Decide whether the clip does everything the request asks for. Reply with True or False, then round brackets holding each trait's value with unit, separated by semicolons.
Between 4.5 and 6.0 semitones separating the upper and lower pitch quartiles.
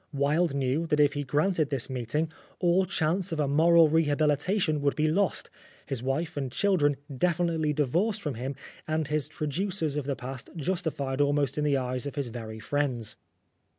False (3.1 semitones)